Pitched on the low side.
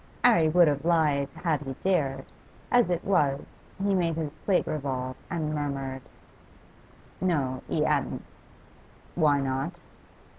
No: medium, 150 Hz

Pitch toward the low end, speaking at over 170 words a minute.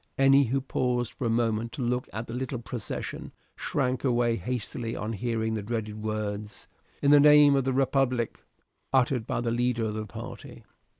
Yes: low, 120 Hz; average, 180 wpm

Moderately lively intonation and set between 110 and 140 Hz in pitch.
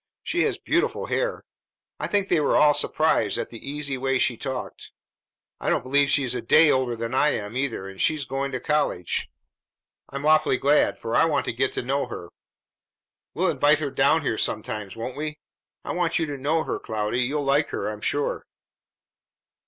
Yes: average, 3.6 semitones; low, 135 Hz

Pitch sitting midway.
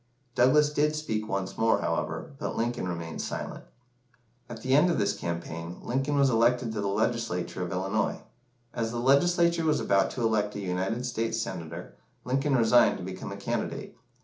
No: low, 115 Hz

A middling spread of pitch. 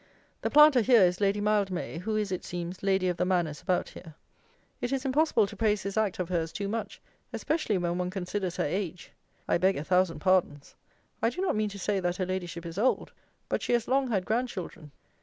Yes: average, 3.5 semitones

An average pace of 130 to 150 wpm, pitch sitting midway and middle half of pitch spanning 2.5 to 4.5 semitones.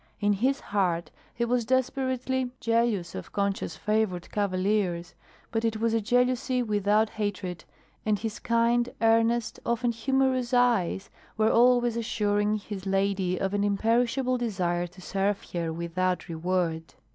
No: slow, 135 wpm; high, 215 Hz; average, 4.0 semitones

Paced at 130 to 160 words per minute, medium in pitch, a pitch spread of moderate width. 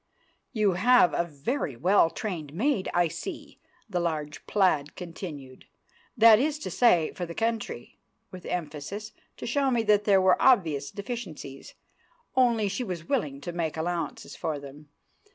No: average, 150 wpm; medium, 180 Hz; wide, 6.1 semitones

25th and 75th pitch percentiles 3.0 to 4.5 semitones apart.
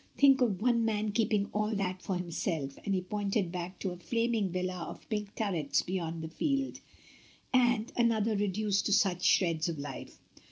Yes: average, 3.6 semitones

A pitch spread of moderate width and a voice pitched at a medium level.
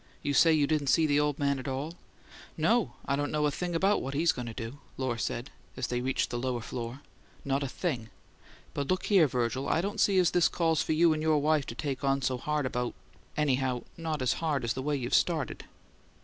Yes: average, 3.6 semitones; medium, 145 Hz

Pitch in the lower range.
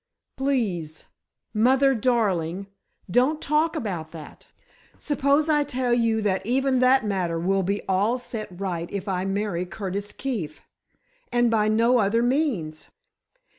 No: high, 215 Hz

